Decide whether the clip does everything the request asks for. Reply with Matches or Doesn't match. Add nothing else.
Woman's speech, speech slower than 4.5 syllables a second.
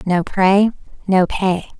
Matches